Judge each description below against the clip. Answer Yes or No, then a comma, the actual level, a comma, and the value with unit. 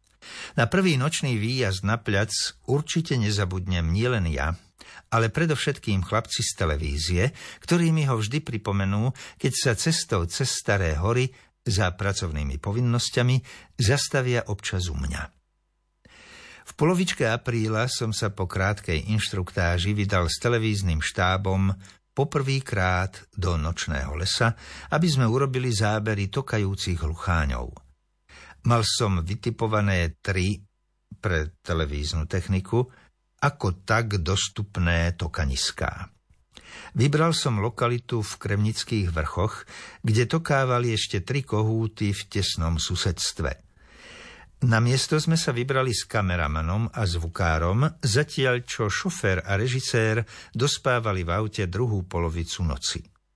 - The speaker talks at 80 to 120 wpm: Yes, slow, 110 wpm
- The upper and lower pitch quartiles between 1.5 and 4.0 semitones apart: No, average, 5.1 semitones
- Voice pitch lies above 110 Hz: No, low, 105 Hz